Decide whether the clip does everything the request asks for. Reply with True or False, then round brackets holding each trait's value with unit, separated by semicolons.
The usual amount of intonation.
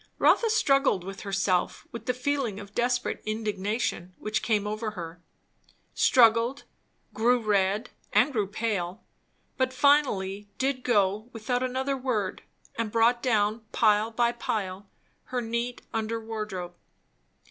True (3.4 semitones)